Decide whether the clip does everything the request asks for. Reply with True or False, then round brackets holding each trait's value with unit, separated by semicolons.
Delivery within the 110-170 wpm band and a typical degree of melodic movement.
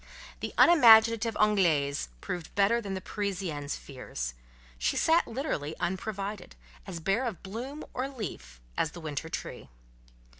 False (135 wpm; 6.3 semitones)